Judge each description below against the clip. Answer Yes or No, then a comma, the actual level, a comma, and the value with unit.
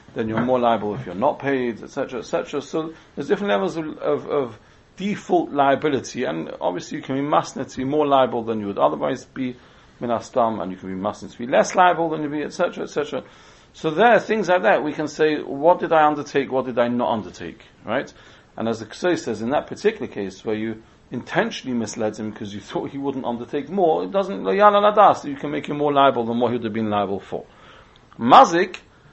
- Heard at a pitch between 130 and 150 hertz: Yes, medium, 140 Hz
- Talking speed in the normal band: No, fast, 210 wpm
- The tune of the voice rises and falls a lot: Yes, wide, 5.9 semitones